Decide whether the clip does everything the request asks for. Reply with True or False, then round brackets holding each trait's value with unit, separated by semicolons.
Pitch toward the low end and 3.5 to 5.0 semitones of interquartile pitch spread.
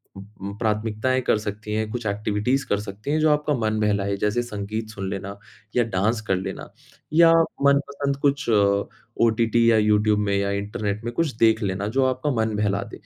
False (110 Hz; 3.1 semitones)